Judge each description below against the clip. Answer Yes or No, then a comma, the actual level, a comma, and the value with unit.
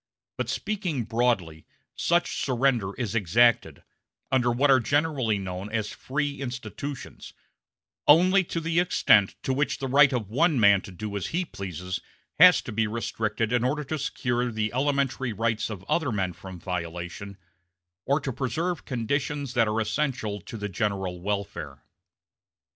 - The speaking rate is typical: Yes, average, 155 wpm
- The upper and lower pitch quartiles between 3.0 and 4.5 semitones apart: No, wide, 5.5 semitones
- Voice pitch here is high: No, low, 120 Hz